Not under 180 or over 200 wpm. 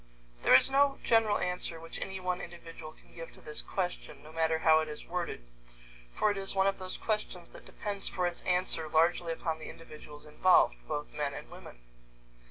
Yes: average, 195 wpm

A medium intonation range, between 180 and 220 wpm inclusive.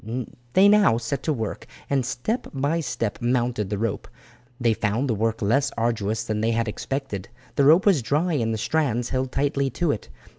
Yes: average, 4.1 semitones; average, 190 wpm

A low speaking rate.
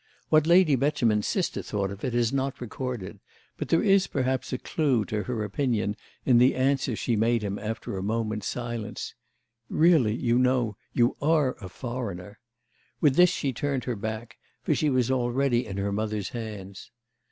No: average, 175 wpm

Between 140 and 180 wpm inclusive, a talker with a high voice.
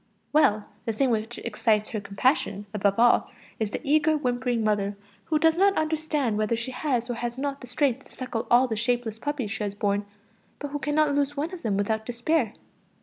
No: fast, 205 wpm; high, 240 Hz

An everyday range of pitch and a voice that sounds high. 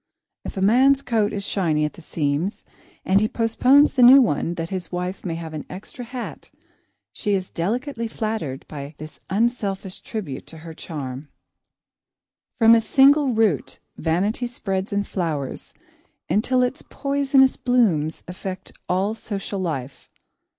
No: wide, 6.2 semitones; high, 195 Hz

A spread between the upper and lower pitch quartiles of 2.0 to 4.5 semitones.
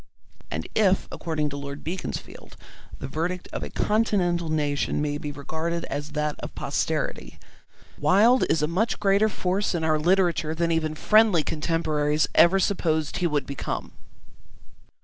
Yes: average, 3.5 semitones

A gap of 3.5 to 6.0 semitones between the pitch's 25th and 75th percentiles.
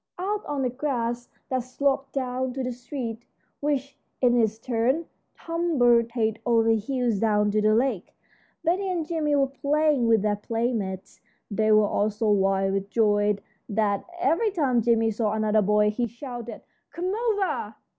Yes: average, 4.4 semitones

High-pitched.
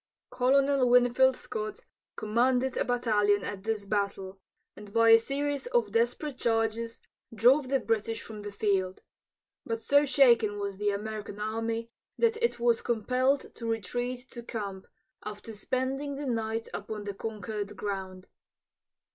Yes: high, 225 Hz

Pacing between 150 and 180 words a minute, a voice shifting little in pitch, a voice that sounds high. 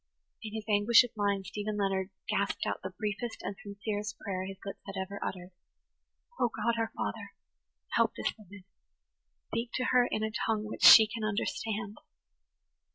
Yes: average, 165 wpm; narrow, 1.9 semitones; high, 210 Hz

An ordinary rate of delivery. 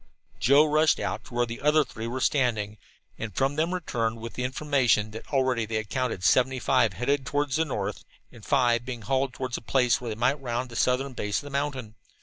No: fast, 215 wpm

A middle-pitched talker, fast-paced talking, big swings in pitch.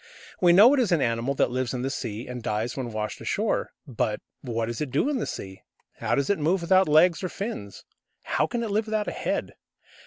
Yes: medium, 145 Hz; fast, 235 wpm; wide, 8.4 semitones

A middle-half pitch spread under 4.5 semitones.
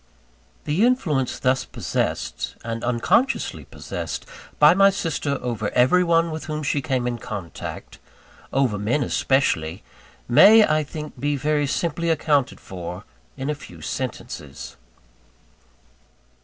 No: average, 5.0 semitones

